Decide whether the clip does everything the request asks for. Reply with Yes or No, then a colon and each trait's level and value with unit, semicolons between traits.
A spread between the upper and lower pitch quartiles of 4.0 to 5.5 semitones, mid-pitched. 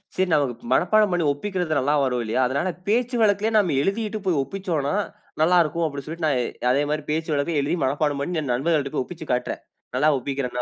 Yes: average, 4.5 semitones; medium, 155 Hz